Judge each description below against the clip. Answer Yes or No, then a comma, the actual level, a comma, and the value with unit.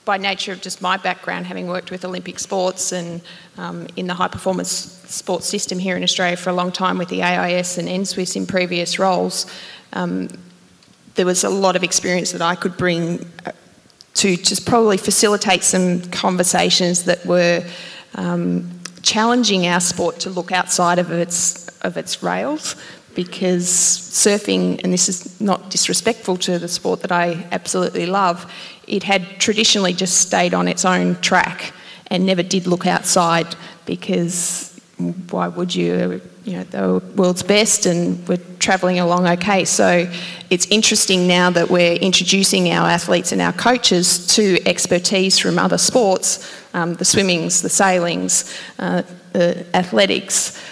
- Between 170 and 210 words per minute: No, average, 155 wpm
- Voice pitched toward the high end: No, medium, 180 Hz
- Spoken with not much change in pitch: Yes, narrow, 1.5 semitones